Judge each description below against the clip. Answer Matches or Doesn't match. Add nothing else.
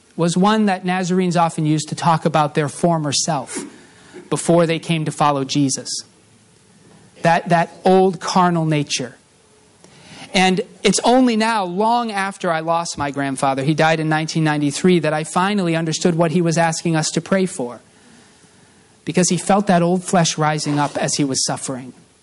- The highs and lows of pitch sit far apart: Doesn't match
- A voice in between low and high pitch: Matches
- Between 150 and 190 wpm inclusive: Matches